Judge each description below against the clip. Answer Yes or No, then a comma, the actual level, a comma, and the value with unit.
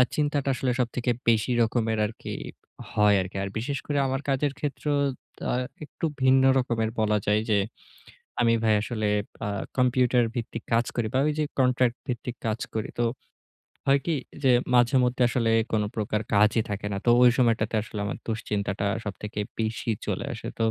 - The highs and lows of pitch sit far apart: No, average, 3.0 semitones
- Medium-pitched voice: No, low, 115 Hz